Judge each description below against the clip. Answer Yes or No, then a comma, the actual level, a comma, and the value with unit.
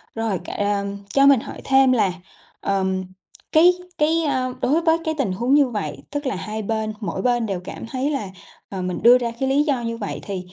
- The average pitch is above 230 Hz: Yes, high, 240 Hz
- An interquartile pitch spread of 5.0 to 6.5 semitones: Yes, wide, 5.4 semitones